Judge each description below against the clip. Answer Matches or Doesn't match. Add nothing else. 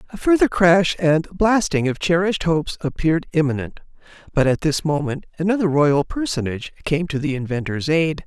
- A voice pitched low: Doesn't match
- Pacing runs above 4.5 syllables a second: Matches